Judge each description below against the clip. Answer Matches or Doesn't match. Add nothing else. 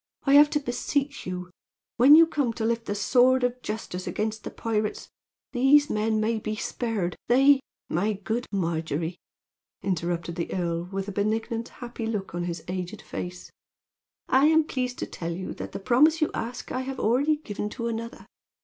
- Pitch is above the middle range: Matches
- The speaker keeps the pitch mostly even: Doesn't match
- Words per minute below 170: Doesn't match